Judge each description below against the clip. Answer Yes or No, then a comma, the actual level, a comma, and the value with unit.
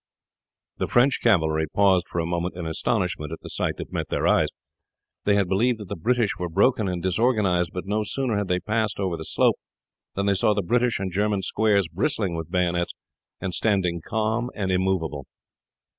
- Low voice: Yes, very low, 95 Hz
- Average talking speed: Yes, average, 190 wpm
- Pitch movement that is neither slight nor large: Yes, average, 3.5 semitones